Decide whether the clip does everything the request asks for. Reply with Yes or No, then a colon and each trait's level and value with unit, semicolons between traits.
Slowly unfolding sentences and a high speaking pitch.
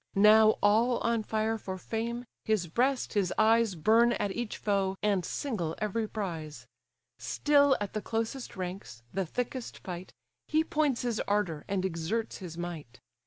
No: average, 155 wpm; high, 210 Hz